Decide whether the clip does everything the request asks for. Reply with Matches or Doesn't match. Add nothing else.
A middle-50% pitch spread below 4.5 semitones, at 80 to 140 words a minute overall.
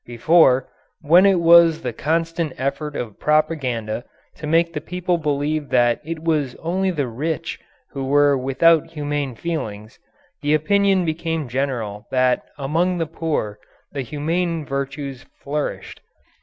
Matches